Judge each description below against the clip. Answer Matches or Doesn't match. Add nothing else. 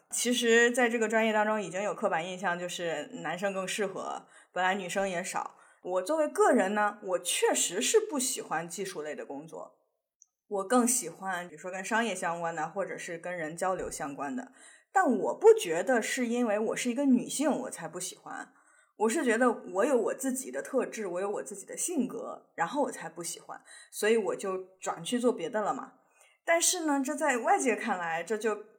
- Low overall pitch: Doesn't match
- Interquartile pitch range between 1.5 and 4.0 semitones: Doesn't match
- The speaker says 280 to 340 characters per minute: Matches